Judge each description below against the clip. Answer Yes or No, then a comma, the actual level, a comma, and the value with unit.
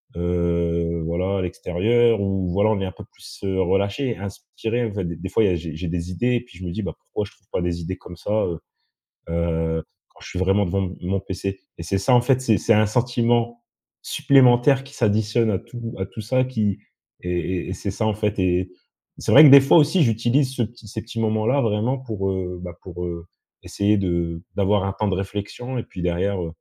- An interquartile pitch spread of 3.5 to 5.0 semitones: Yes, average, 4.6 semitones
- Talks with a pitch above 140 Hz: No, low, 100 Hz